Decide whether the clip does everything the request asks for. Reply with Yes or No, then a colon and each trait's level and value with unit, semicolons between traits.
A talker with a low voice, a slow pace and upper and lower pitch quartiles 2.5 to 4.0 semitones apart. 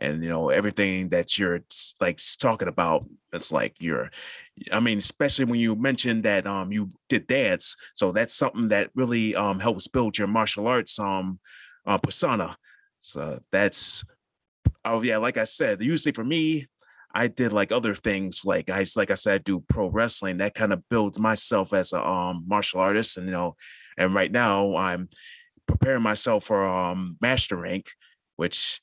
No: low, 100 Hz; average, 175 wpm; average, 3.6 semitones